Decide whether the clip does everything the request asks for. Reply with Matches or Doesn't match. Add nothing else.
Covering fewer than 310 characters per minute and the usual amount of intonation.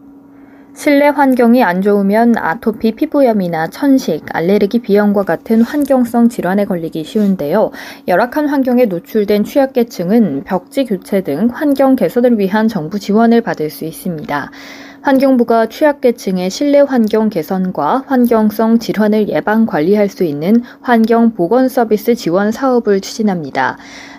Doesn't match